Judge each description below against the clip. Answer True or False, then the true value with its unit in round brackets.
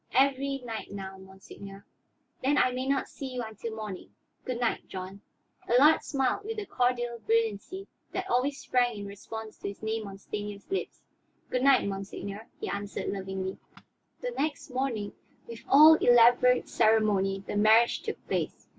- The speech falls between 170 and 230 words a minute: False (155 wpm)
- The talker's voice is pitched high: True (230 Hz)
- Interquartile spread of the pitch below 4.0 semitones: False (4.4 semitones)